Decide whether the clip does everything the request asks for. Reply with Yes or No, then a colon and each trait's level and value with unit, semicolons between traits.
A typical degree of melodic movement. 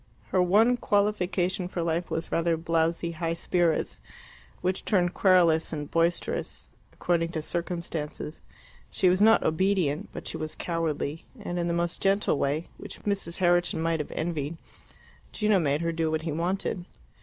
No: narrow, 2.2 semitones